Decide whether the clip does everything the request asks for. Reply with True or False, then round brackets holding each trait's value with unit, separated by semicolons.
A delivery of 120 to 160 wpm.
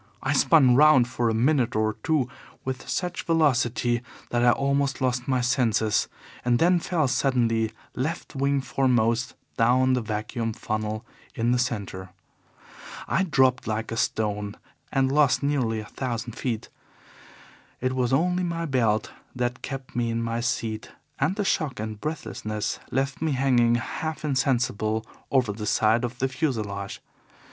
True (150 wpm)